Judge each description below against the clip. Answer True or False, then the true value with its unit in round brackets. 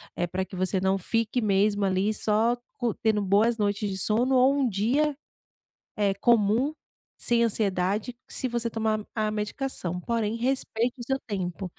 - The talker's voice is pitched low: False (215 Hz)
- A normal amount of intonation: True (3.2 semitones)